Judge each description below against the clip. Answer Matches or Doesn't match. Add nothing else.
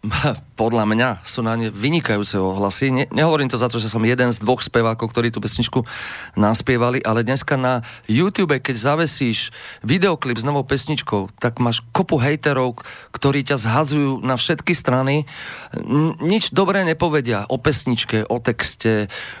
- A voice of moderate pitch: Doesn't match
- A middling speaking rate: Matches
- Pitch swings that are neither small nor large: Matches